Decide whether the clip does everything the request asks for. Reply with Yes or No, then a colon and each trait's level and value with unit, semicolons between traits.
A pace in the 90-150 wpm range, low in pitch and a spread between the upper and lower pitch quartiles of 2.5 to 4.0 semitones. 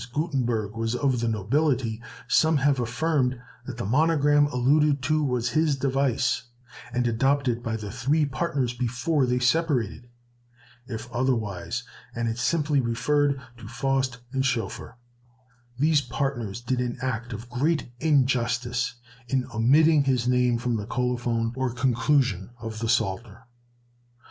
Yes: average, 140 wpm; low, 125 Hz; average, 3.0 semitones